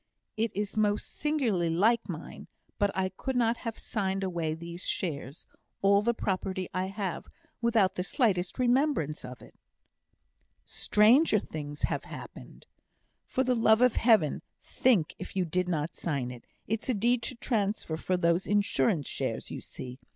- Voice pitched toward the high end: Yes, high, 195 Hz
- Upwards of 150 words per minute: Yes, average, 160 wpm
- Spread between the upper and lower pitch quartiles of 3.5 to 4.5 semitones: No, average, 5.2 semitones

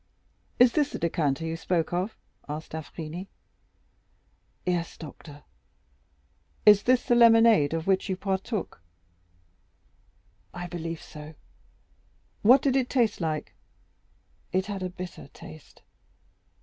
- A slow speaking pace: Yes, slow, 120 wpm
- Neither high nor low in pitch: Yes, medium, 180 Hz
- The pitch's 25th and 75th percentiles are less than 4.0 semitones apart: No, average, 5.1 semitones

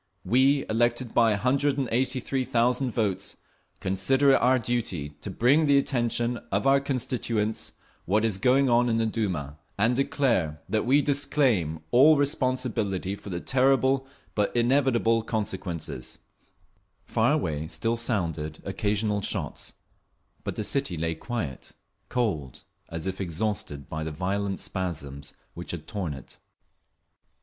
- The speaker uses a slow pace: Yes, slow, 130 wpm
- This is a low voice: Yes, low, 115 Hz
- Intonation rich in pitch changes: Yes, wide, 5.7 semitones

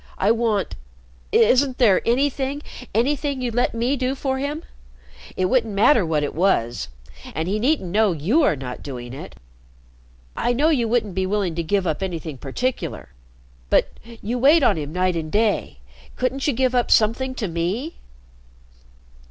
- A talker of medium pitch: No, high, 225 Hz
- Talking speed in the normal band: Yes, average, 165 wpm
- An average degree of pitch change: No, wide, 6.5 semitones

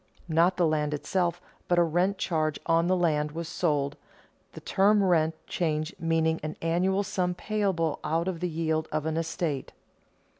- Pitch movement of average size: No, narrow, 2.3 semitones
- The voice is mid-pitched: Yes, medium, 165 Hz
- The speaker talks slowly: No, average, 165 wpm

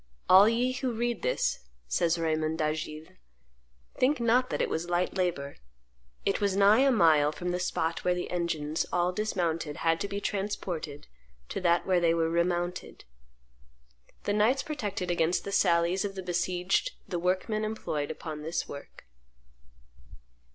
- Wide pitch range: No, average, 3.8 semitones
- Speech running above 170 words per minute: No, average, 155 wpm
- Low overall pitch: No, medium, 180 Hz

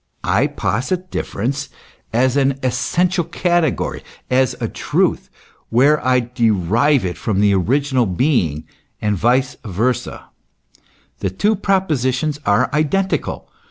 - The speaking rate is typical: No, slow, 115 wpm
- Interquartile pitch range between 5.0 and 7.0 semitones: Yes, average, 5.3 semitones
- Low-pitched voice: Yes, low, 130 Hz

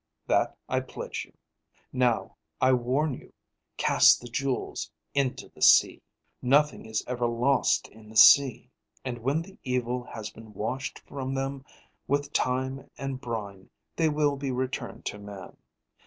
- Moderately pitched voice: No, low, 130 Hz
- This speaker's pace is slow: No, average, 150 wpm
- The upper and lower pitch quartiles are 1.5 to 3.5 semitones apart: Yes, average, 2.7 semitones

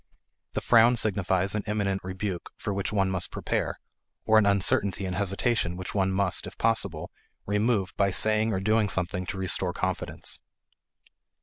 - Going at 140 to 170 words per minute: Yes, average, 160 wpm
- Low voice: Yes, low, 100 Hz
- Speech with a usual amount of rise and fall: No, narrow, 2.2 semitones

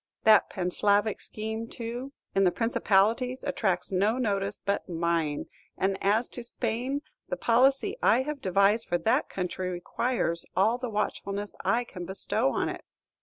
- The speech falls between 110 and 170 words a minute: Yes, average, 150 wpm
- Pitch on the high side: Yes, high, 215 Hz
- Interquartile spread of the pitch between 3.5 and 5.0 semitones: Yes, average, 4.1 semitones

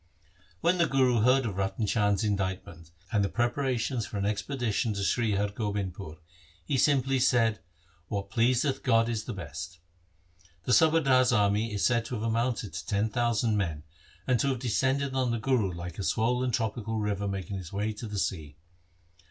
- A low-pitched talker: Yes, low, 110 Hz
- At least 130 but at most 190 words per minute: Yes, average, 185 wpm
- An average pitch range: Yes, average, 3.9 semitones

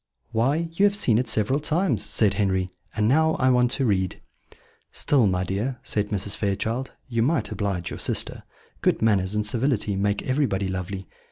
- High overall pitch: No, low, 110 Hz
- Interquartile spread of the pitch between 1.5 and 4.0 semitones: No, average, 4.9 semitones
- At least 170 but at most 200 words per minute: Yes, average, 175 wpm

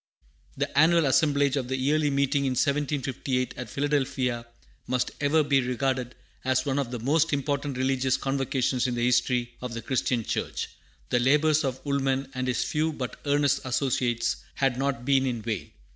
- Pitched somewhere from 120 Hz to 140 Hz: Yes, low, 135 Hz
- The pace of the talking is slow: No, average, 170 wpm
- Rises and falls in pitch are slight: Yes, narrow, 2.1 semitones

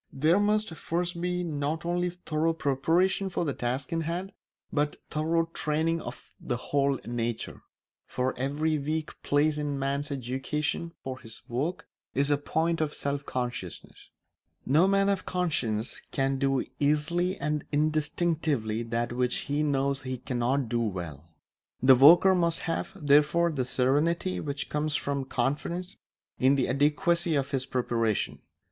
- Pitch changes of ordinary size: Yes, average, 4.0 semitones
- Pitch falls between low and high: Yes, medium, 145 Hz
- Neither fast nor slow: Yes, average, 150 wpm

